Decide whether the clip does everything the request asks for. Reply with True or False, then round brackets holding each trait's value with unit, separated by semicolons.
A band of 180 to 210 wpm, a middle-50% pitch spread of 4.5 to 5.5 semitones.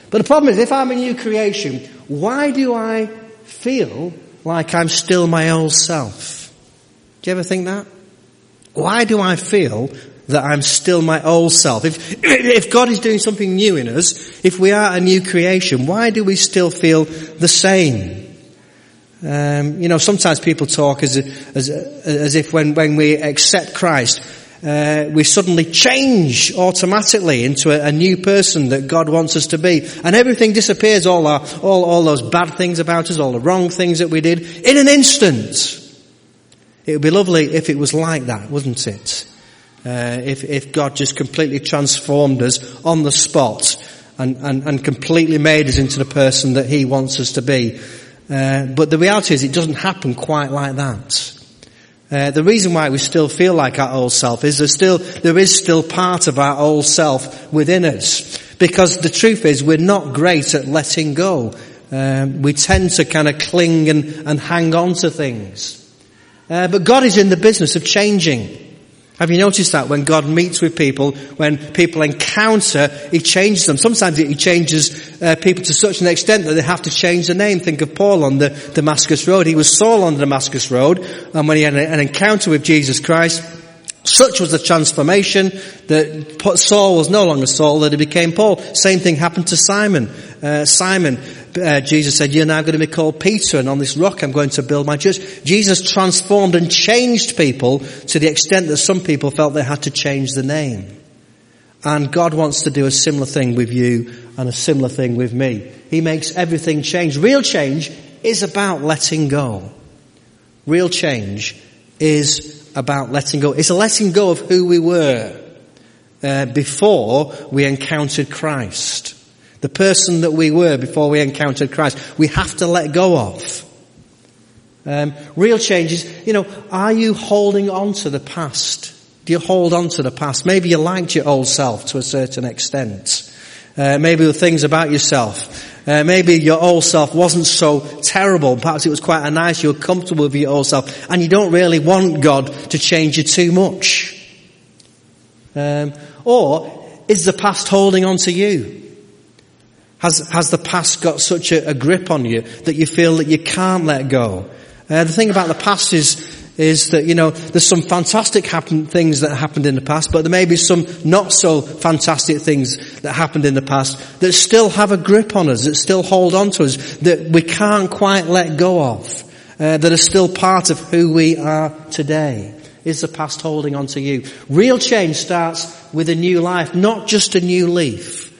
False (190 wpm; 3.9 semitones)